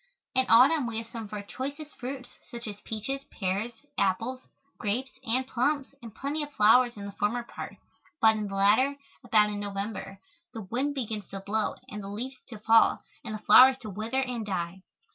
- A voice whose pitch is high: Yes, high, 225 Hz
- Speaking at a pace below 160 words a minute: No, average, 195 wpm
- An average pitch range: Yes, average, 3.8 semitones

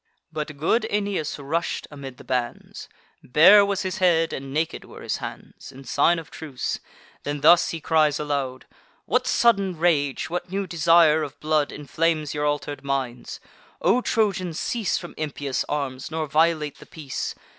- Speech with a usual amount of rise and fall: Yes, average, 3.4 semitones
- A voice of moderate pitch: Yes, medium, 155 Hz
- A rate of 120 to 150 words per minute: No, average, 160 wpm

